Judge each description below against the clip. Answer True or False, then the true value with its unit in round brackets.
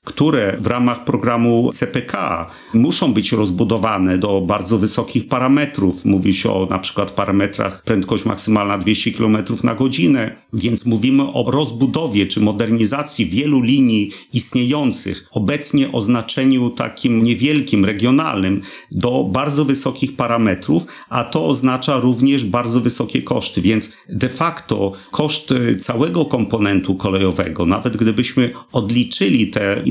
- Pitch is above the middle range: False (120 Hz)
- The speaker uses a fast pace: False (120 wpm)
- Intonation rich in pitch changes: False (4.0 semitones)